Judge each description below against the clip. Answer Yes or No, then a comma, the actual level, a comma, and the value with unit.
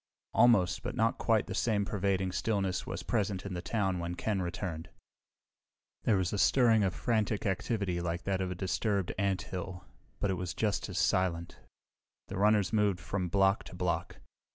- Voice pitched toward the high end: No, very low, 95 Hz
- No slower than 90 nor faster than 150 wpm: No, average, 175 wpm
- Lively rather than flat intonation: No, narrow, 2.6 semitones